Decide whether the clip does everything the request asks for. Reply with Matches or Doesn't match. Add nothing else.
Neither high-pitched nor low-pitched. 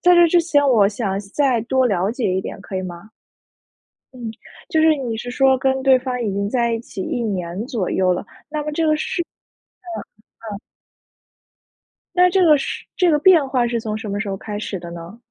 Doesn't match